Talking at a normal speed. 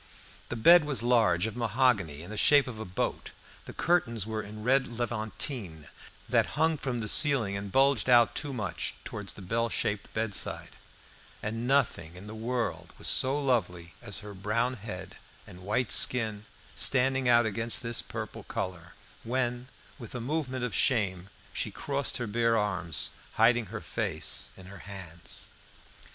Yes: average, 165 wpm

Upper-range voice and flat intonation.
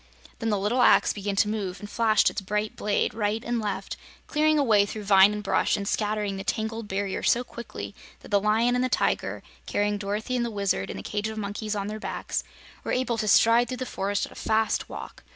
Yes: high, 210 Hz; narrow, 2.1 semitones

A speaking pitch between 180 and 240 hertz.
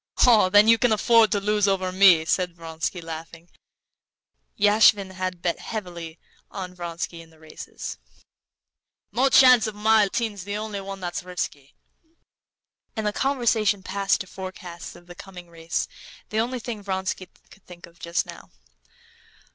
Yes: high, 190 Hz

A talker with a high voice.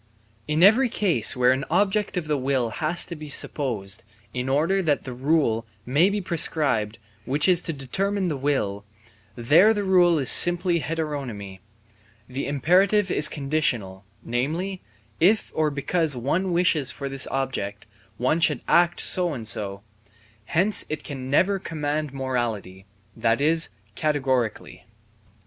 No: medium, 145 Hz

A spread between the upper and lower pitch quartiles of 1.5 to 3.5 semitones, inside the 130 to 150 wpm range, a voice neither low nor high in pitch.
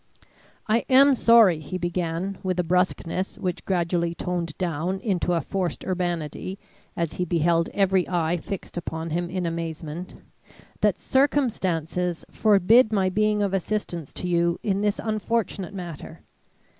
Yes: average, 2.8 semitones; average, 140 wpm; medium, 180 Hz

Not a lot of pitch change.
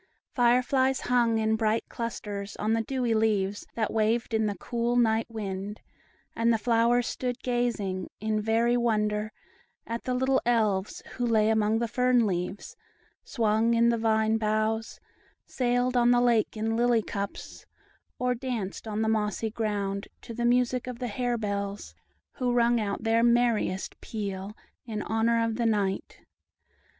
Yes: narrow, 2.1 semitones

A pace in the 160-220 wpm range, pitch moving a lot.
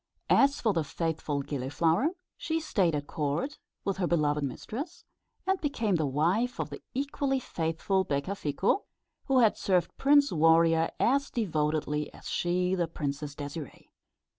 No: average, 140 wpm; wide, 8.3 semitones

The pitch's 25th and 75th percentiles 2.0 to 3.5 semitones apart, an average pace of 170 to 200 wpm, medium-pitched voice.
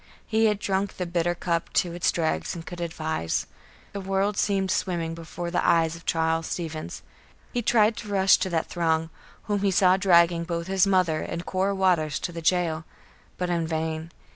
Yes: average, 2.7 semitones; average, 190 wpm; medium, 175 Hz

